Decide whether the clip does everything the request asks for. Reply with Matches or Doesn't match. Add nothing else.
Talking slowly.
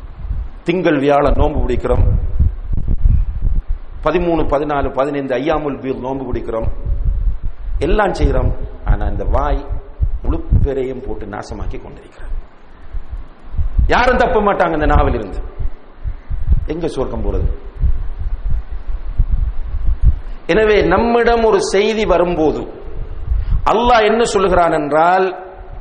Matches